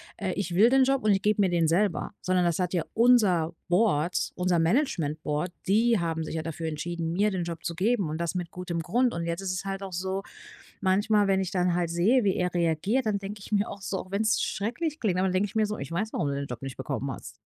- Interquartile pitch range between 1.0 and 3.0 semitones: No, average, 3.6 semitones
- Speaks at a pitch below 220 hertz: Yes, medium, 185 Hz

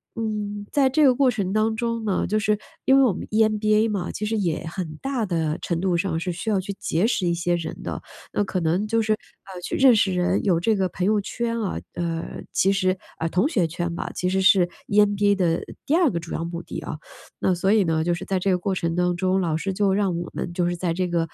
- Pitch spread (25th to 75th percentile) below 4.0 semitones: Yes, average, 3.5 semitones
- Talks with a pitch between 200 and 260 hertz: No, high, 190 Hz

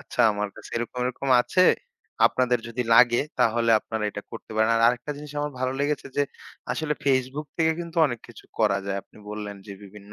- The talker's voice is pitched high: No, low, 120 Hz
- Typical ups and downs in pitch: Yes, average, 4.7 semitones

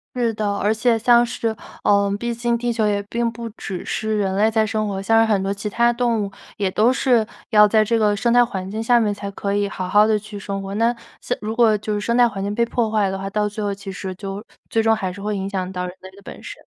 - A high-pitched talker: Yes, high, 210 Hz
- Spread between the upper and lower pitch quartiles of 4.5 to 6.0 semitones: No, narrow, 2.4 semitones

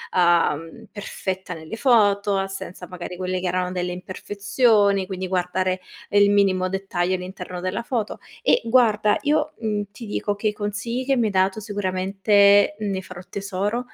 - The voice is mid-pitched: No, high, 195 Hz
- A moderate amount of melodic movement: No, narrow, 2.2 semitones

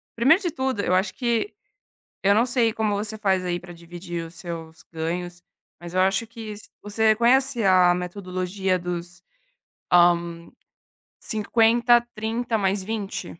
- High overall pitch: Yes, high, 195 Hz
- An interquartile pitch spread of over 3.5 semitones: Yes, average, 4.2 semitones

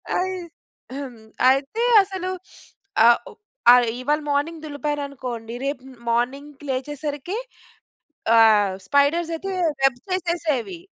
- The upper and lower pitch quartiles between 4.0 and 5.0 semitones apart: Yes, average, 4.7 semitones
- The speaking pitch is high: Yes, very high, 285 Hz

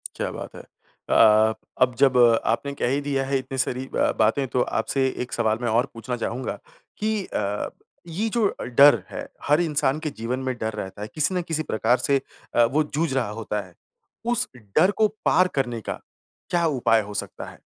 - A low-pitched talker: Yes, low, 130 Hz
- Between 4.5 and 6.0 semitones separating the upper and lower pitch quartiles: Yes, average, 4.8 semitones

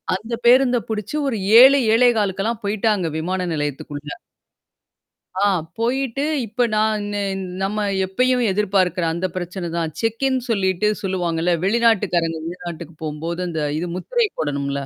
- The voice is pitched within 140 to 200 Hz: Yes, high, 195 Hz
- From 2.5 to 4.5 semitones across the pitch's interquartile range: No, average, 5.0 semitones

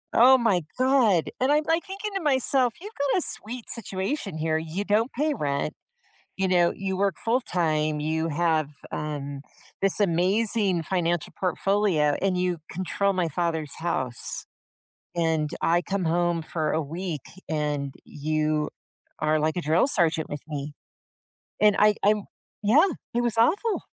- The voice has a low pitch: No, medium, 180 Hz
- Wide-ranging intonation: Yes, wide, 6.2 semitones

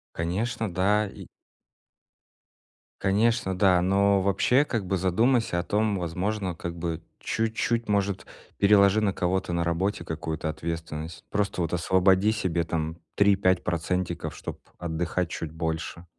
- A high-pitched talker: No, very low, 95 Hz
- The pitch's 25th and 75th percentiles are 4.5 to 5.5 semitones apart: No, average, 3.2 semitones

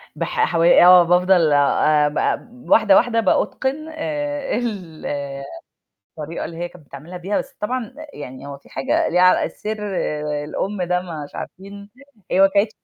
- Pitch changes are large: Yes, wide, 6.1 semitones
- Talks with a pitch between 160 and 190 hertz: Yes, medium, 185 Hz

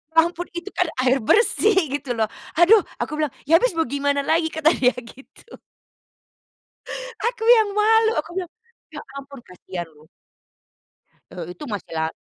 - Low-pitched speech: No, very high, 305 Hz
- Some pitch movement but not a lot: No, wide, 7.1 semitones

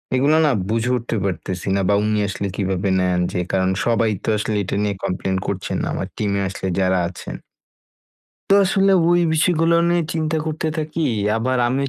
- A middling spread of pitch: No, wide, 8.3 semitones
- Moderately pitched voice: No, low, 115 Hz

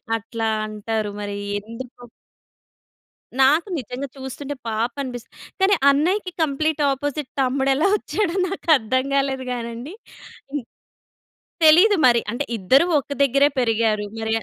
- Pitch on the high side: Yes, very high, 265 Hz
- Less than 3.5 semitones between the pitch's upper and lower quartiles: No, average, 4.1 semitones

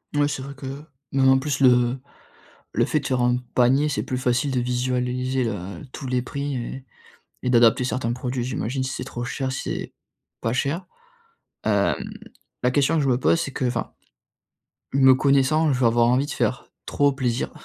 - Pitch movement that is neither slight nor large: No, narrow, 1.9 semitones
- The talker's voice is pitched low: Yes, low, 130 Hz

